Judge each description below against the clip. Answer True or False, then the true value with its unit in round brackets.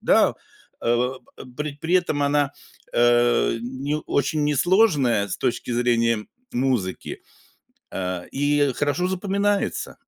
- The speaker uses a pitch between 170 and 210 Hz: False (140 Hz)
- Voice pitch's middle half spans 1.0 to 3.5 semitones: False (3.9 semitones)